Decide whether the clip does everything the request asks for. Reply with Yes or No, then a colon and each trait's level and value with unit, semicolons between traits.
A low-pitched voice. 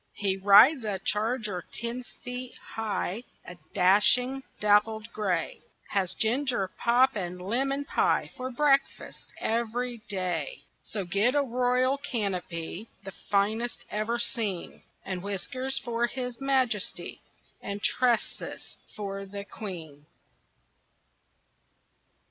No: high, 220 Hz